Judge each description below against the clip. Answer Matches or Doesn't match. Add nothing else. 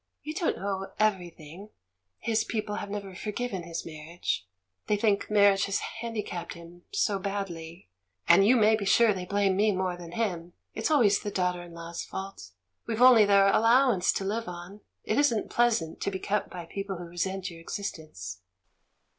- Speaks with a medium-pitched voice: Doesn't match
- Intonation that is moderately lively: Matches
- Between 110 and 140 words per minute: Doesn't match